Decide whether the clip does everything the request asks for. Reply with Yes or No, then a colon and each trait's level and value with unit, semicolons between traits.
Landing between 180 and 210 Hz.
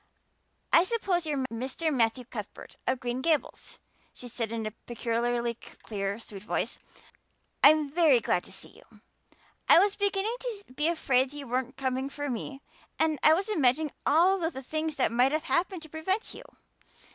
No: very high, 280 Hz